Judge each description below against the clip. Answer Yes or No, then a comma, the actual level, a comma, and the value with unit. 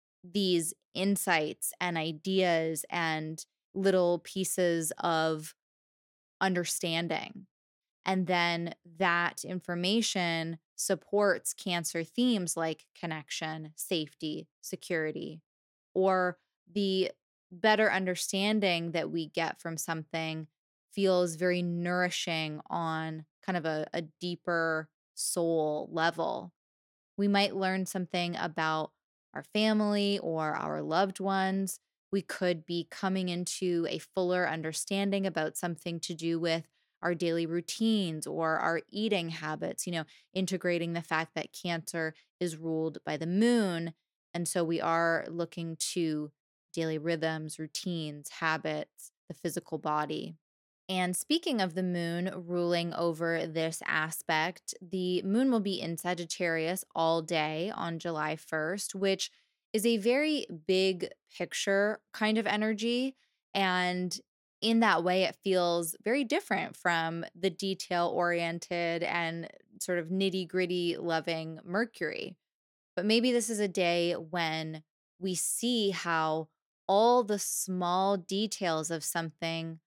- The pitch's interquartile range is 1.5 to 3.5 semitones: Yes, average, 2.7 semitones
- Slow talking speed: Yes, slow, 120 wpm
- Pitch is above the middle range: No, medium, 175 Hz